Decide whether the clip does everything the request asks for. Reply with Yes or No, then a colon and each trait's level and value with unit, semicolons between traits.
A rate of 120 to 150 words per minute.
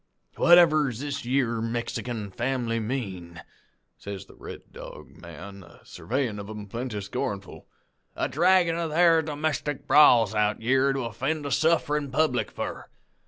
Yes: average, 145 wpm